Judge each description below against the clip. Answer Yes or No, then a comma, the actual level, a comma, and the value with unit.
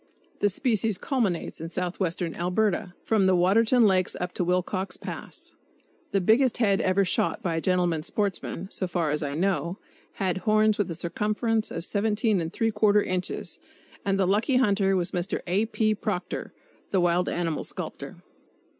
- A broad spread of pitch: No, average, 3.2 semitones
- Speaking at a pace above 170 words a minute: No, average, 155 wpm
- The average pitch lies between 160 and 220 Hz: Yes, high, 190 Hz